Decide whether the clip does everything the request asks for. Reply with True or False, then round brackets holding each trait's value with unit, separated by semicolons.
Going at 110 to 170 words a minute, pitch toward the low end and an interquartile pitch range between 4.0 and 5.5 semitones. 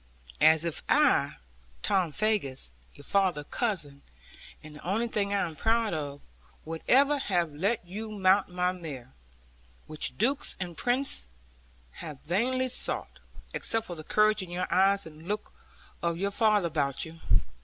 False (155 wpm; 185 Hz; 5.2 semitones)